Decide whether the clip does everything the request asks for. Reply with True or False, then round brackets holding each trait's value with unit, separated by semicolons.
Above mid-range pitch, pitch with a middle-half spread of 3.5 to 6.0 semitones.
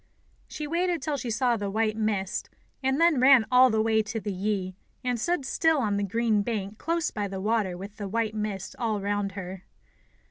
True (220 Hz; 4.0 semitones)